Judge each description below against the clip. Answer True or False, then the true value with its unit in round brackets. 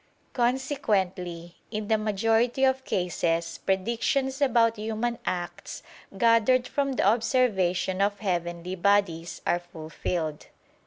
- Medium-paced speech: False (105 wpm)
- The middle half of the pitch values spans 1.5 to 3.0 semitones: False (5.2 semitones)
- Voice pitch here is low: False (210 Hz)